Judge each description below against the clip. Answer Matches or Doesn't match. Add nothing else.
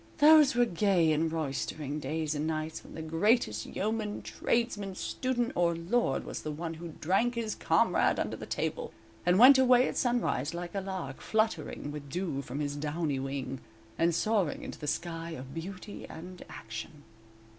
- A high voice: Doesn't match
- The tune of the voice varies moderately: Doesn't match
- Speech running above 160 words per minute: Matches